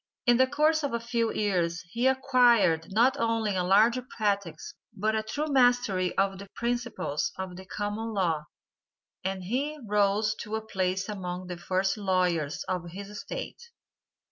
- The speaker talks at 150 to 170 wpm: Yes, average, 160 wpm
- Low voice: No, high, 205 Hz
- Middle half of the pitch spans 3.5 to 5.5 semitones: Yes, average, 4.1 semitones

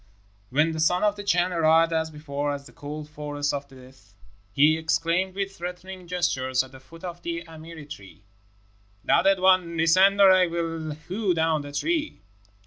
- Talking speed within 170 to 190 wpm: Yes, average, 180 wpm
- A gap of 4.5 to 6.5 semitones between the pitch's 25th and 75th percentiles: No, average, 3.7 semitones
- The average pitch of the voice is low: No, medium, 165 Hz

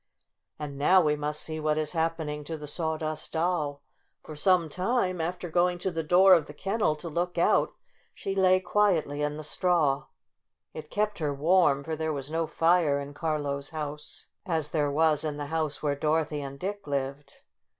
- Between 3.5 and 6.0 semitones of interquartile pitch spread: No, average, 3.0 semitones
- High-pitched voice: No, medium, 155 Hz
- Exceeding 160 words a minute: Yes, average, 190 wpm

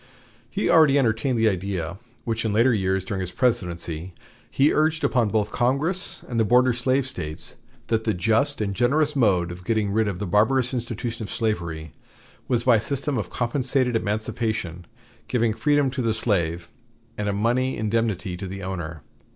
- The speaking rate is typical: Yes, average, 175 wpm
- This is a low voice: Yes, low, 110 Hz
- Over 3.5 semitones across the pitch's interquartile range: Yes, average, 4.7 semitones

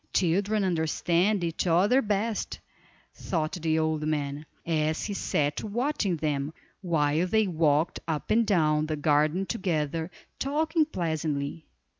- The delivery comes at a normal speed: No, slow, 125 wpm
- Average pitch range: Yes, average, 4.4 semitones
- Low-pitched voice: No, medium, 165 Hz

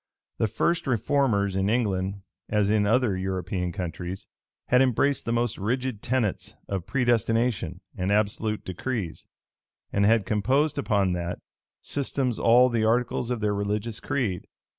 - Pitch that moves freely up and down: No, average, 4.2 semitones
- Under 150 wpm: Yes, average, 140 wpm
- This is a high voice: No, low, 110 Hz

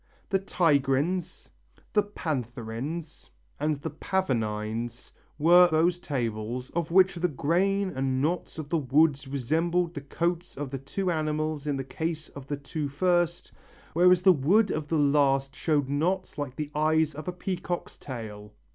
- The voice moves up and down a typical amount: Yes, average, 4.2 semitones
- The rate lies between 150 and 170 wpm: Yes, average, 155 wpm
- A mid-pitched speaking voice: Yes, medium, 155 Hz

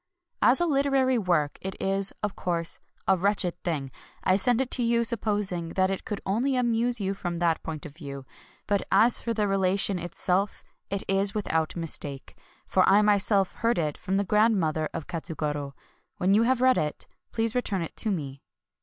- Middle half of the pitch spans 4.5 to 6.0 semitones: Yes, average, 4.9 semitones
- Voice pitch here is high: Yes, high, 195 Hz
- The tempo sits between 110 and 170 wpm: No, average, 185 wpm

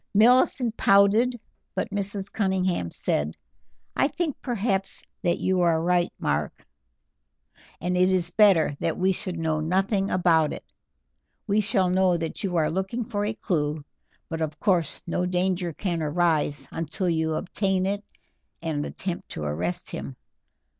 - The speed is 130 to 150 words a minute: Yes, average, 145 wpm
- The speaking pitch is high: No, medium, 180 Hz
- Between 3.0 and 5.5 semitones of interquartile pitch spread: Yes, average, 3.5 semitones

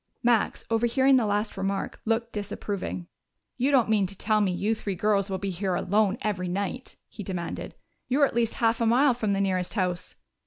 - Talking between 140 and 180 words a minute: No, average, 195 wpm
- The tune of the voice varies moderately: Yes, average, 3.1 semitones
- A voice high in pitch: Yes, high, 210 Hz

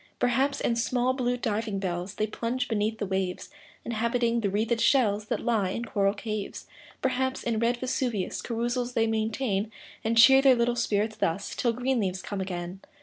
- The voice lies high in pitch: Yes, high, 225 Hz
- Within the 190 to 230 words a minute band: No, average, 175 wpm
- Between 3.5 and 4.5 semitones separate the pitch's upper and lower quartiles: No, average, 3.1 semitones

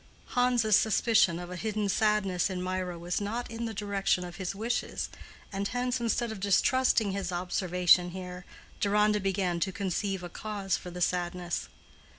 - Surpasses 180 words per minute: No, average, 160 wpm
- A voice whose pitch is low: No, high, 195 Hz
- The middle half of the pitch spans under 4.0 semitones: Yes, average, 3.1 semitones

